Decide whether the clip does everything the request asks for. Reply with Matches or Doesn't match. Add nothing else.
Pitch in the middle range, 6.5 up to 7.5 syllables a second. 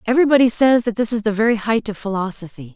Doesn't match